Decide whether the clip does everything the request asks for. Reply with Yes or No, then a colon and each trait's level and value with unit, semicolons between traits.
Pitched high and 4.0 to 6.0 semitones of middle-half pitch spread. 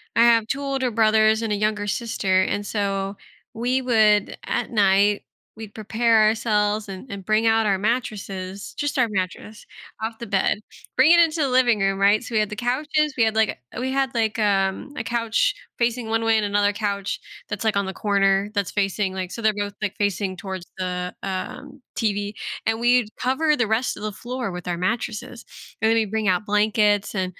No: high, 215 Hz; average, 2.7 semitones